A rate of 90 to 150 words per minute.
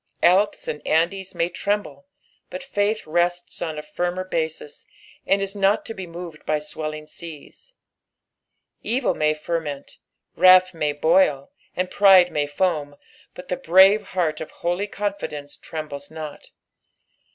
Yes: average, 140 wpm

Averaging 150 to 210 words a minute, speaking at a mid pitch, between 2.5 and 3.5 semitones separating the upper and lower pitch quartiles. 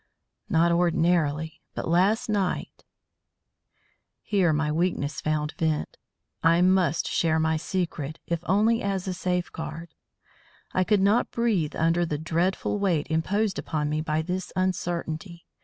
No: slow, 135 wpm; medium, 170 Hz; average, 2.9 semitones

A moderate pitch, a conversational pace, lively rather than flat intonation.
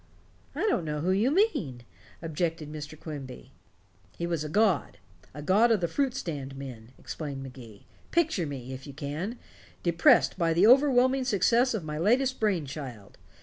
Yes: medium, 165 Hz; average, 165 wpm; wide, 8.0 semitones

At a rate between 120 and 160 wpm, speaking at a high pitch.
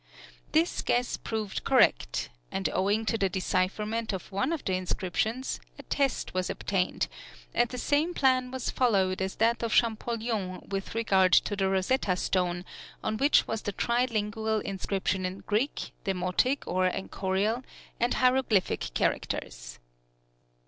Yes: average, 140 wpm; high, 210 Hz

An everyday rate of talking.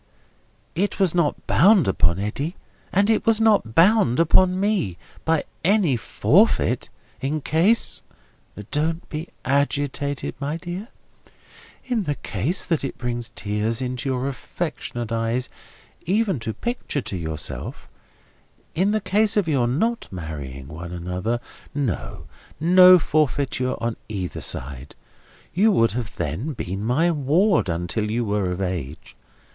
No: slow, 130 wpm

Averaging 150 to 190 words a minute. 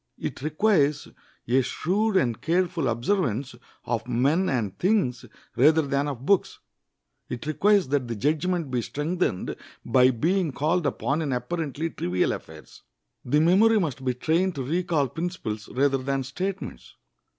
No: average, 140 wpm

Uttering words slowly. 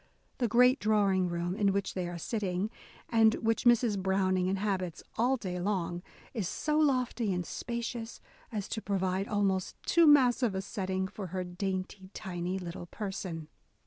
No: average, 155 wpm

